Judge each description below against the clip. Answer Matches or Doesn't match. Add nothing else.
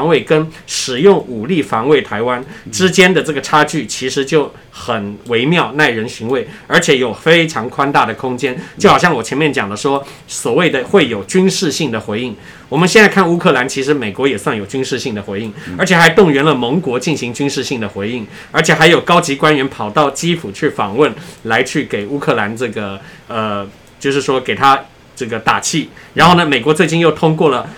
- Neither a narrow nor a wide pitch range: Matches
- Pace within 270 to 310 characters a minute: Matches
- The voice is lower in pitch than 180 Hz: Matches